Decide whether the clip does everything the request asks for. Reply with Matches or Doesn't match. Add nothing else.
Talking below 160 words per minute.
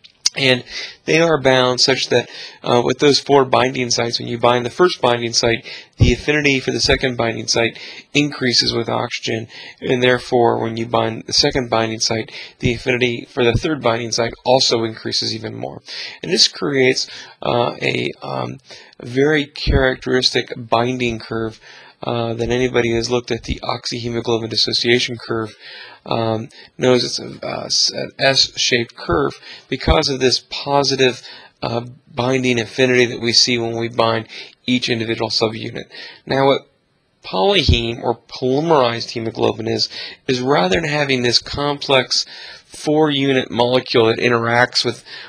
Matches